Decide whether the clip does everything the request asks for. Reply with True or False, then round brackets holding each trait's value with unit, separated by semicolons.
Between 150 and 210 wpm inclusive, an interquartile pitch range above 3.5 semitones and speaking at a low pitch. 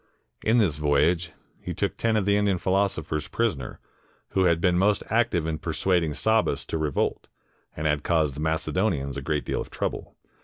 True (180 wpm; 4.7 semitones; 85 Hz)